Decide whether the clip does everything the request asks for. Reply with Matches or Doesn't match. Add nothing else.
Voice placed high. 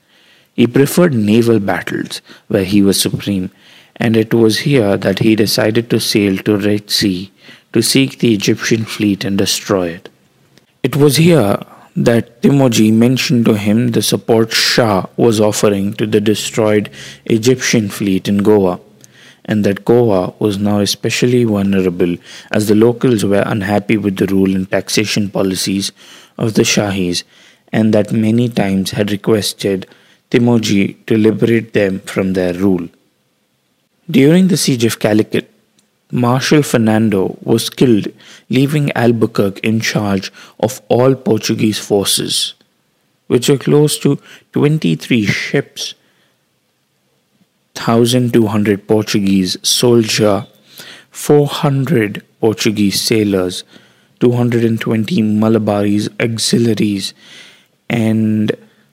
Doesn't match